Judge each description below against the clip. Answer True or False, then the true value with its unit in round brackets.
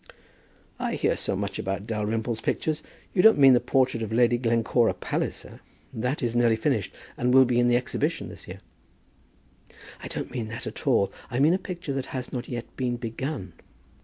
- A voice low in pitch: True (120 Hz)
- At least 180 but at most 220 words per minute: True (190 wpm)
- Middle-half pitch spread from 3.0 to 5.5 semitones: False (2.6 semitones)